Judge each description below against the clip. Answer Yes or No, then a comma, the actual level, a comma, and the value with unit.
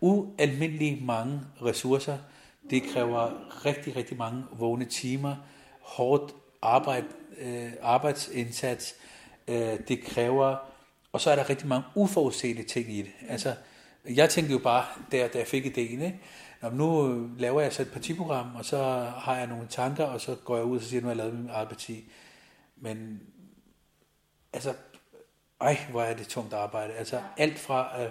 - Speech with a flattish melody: No, average, 3.5 semitones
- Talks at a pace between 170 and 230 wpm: No, average, 160 wpm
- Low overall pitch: Yes, low, 130 Hz